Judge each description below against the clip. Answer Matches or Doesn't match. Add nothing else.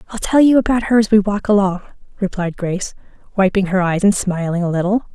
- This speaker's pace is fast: Matches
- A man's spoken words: Doesn't match